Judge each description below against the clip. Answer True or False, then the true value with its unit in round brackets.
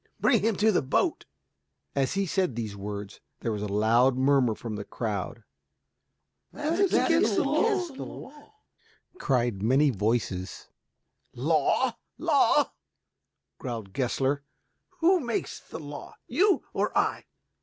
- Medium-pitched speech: False (130 Hz)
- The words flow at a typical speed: False (125 wpm)